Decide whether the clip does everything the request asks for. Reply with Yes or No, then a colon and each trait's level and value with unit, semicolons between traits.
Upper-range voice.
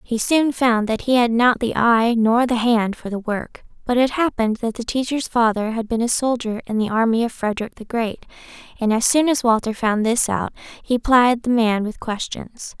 Yes: high, 230 Hz